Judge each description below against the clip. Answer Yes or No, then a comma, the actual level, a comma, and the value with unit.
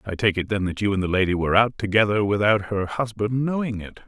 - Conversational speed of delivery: No, fast, 250 wpm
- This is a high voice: No, low, 105 Hz